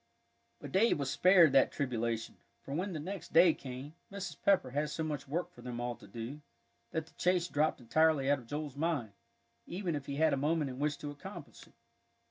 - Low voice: No, medium, 150 Hz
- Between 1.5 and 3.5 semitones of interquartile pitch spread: No, average, 3.9 semitones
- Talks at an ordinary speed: No, fast, 210 wpm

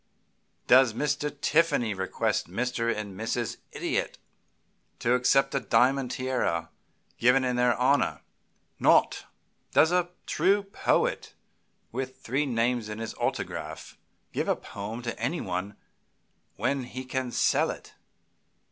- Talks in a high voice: No, low, 125 Hz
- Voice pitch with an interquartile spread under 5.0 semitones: Yes, average, 3.1 semitones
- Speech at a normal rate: No, slow, 120 wpm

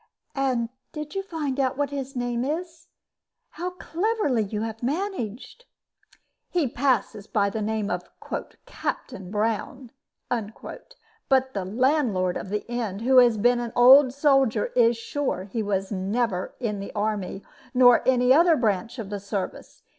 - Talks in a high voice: Yes, high, 245 Hz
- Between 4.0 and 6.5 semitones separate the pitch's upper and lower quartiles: Yes, average, 4.8 semitones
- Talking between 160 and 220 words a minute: No, average, 145 wpm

